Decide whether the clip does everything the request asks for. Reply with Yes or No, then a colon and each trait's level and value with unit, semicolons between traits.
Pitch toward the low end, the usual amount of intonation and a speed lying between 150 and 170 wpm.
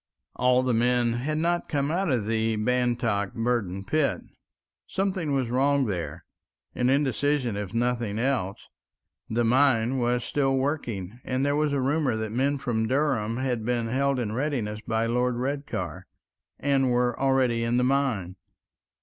Yes: low, 125 Hz; average, 3.5 semitones; average, 155 wpm